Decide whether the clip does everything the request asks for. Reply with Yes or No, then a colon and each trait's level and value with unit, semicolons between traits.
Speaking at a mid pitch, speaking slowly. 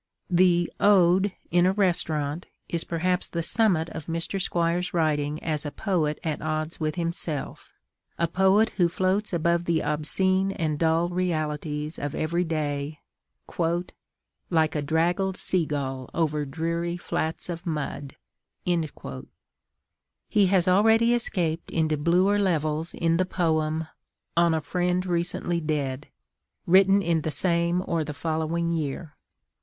Yes: medium, 170 Hz; slow, 130 wpm